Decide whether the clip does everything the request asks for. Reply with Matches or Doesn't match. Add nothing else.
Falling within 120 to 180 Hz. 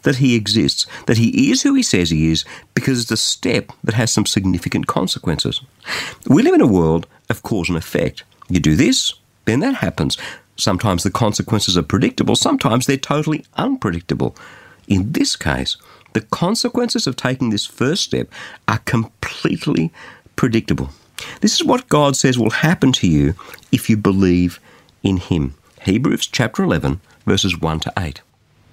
Doesn't match